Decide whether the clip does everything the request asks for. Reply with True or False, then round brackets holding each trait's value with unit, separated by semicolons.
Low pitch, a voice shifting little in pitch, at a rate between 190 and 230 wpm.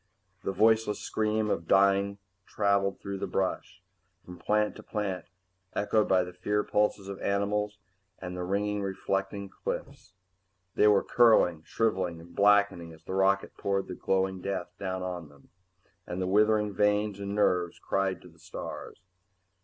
False (100 Hz; 2.1 semitones; 160 wpm)